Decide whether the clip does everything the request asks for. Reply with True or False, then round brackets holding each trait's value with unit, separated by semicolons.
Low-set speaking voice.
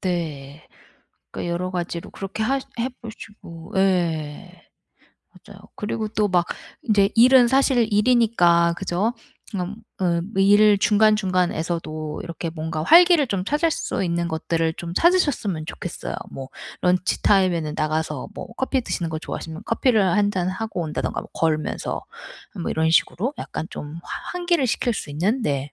False (185 Hz)